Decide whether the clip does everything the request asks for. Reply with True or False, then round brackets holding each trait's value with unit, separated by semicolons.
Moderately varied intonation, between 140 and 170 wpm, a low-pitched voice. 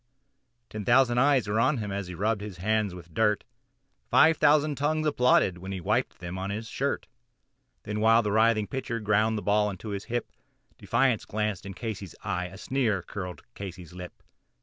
False (3.6 semitones; 185 wpm; 105 Hz)